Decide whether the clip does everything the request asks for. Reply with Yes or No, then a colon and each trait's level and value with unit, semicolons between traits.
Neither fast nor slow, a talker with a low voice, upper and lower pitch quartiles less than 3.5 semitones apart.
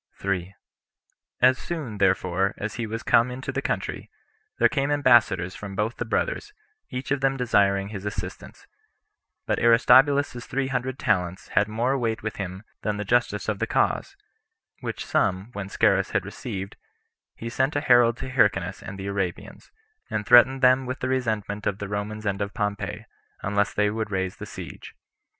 No: average, 170 wpm; low, 110 Hz; average, 4.2 semitones